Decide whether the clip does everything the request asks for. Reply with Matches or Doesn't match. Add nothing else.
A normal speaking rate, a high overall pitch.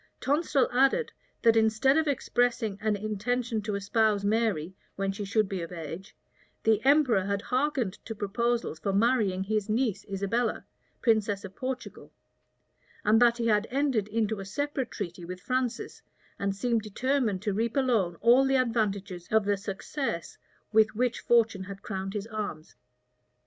Matches